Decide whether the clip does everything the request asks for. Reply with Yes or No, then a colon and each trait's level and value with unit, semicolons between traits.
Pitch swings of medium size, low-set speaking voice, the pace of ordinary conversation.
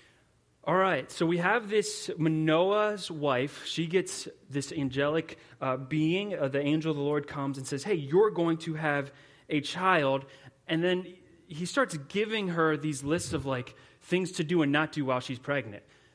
No: average, 3.9 semitones; medium, 155 Hz; average, 180 wpm